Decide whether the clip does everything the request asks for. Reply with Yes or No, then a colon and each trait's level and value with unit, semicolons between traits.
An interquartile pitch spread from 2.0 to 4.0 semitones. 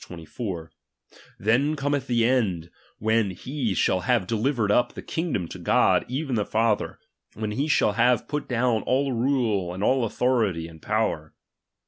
No: average, 4.5 semitones